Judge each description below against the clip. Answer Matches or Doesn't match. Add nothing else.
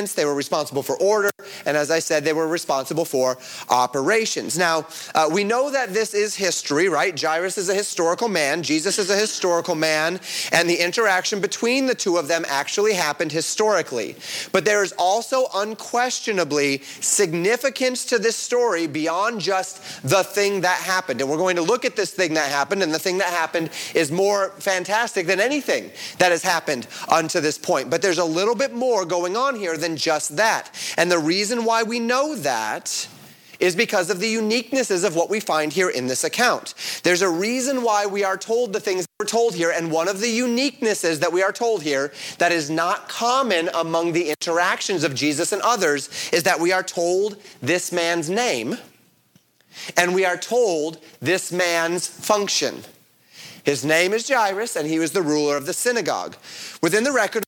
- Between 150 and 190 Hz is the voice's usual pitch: Matches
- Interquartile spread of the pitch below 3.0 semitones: Doesn't match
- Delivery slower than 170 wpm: Doesn't match